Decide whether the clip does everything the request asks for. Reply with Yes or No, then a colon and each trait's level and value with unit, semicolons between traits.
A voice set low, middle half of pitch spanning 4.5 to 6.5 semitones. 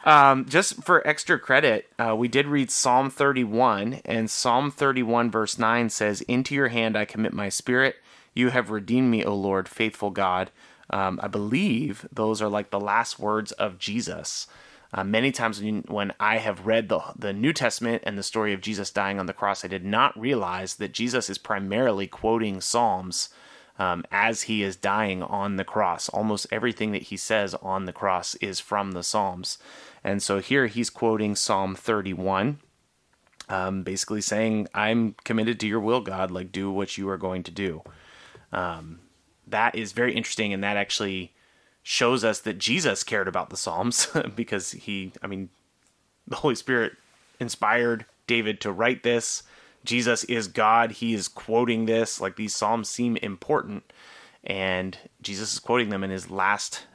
No: low, 110 Hz; average, 3.2 semitones